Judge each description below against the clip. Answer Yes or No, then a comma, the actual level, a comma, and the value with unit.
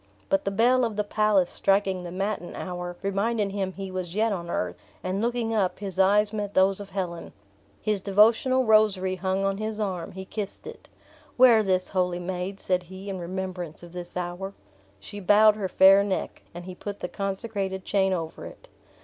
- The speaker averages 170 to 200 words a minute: Yes, average, 190 wpm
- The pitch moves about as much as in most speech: No, narrow, 2.2 semitones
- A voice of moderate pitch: No, high, 195 Hz